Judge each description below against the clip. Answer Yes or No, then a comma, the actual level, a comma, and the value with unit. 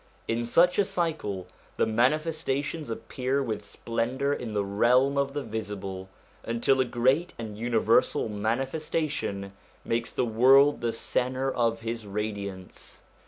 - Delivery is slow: Yes, slow, 130 wpm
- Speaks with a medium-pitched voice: No, low, 120 Hz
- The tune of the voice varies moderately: Yes, average, 4.1 semitones